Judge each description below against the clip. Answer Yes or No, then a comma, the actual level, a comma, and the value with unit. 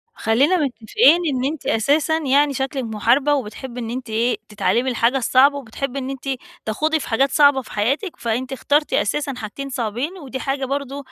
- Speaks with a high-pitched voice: Yes, very high, 265 Hz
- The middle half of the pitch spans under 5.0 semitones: Yes, average, 3.3 semitones